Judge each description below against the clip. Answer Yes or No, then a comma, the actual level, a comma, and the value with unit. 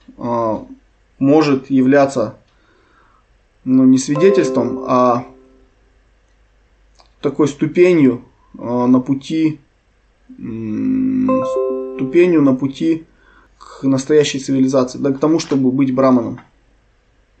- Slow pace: Yes, slow, 75 wpm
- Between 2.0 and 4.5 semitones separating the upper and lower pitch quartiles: Yes, average, 3.2 semitones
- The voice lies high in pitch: No, low, 135 Hz